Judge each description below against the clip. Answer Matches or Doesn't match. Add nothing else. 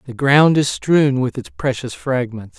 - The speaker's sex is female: Doesn't match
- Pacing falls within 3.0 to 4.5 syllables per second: Matches